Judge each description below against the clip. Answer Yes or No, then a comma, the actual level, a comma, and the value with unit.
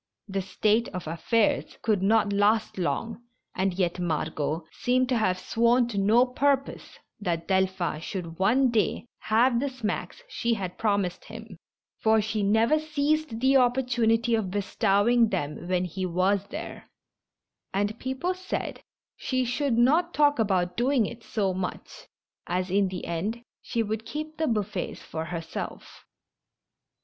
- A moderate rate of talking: Yes, average, 150 wpm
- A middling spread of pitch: Yes, average, 4.7 semitones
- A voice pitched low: No, high, 215 Hz